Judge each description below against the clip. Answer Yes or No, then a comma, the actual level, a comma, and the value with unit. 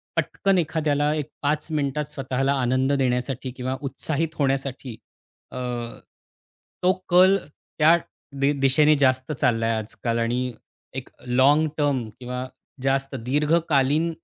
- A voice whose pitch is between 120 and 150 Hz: Yes, medium, 140 Hz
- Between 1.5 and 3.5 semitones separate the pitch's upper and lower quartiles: Yes, average, 2.8 semitones